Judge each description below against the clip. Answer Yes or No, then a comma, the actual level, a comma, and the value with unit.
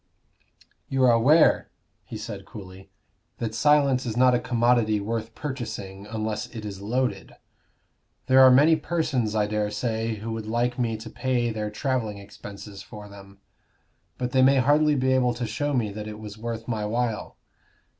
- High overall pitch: No, low, 115 Hz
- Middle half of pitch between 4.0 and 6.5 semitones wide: No, average, 3.3 semitones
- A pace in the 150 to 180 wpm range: Yes, average, 170 wpm